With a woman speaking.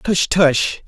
No: male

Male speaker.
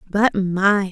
No: female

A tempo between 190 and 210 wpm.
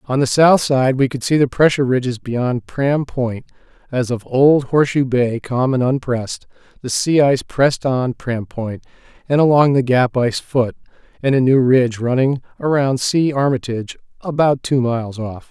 No: average, 170 wpm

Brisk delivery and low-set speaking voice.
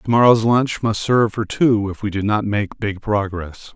Yes: fast, 225 wpm; low, 105 Hz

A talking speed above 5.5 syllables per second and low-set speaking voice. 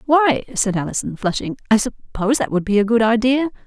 No: 5.7 syllables/s; high, 230 Hz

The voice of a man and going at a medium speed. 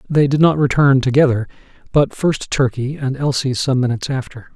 Yes: male; average, 170 wpm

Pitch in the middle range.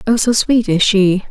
No: high, 210 Hz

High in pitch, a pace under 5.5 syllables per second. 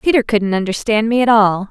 No: high, 220 Hz; 5.6 syllables/s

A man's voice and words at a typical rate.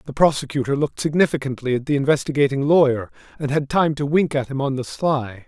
Yes: male; average, 195 wpm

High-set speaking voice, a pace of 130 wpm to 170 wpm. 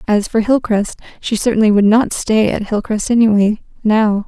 Yes: high, 215 Hz; average, 140 wpm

